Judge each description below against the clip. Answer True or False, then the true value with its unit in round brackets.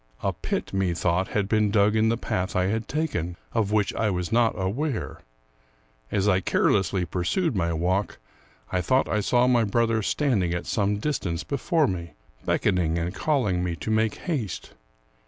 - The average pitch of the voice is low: True (100 Hz)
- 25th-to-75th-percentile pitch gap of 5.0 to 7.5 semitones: False (4.2 semitones)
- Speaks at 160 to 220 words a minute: True (170 wpm)